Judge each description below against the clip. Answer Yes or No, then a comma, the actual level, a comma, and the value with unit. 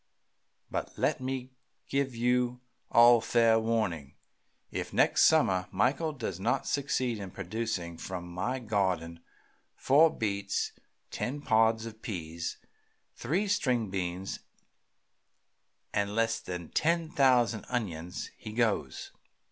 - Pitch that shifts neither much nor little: Yes, average, 5.0 semitones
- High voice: No, low, 115 Hz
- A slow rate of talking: Yes, slow, 115 wpm